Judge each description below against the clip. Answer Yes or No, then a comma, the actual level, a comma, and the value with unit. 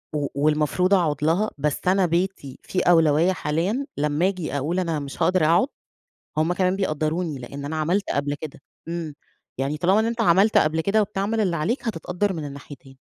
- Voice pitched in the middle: Yes, medium, 165 Hz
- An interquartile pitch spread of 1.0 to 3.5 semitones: No, average, 4.0 semitones